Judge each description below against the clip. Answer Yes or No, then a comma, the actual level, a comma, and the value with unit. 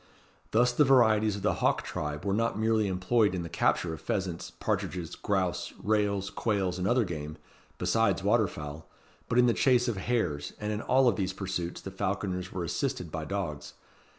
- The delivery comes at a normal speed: Yes, average, 185 wpm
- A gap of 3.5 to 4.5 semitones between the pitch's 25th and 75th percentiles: Yes, average, 3.9 semitones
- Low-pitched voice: Yes, low, 100 Hz